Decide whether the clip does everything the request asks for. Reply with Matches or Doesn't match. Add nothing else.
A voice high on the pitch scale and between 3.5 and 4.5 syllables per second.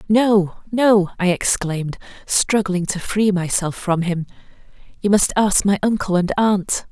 Matches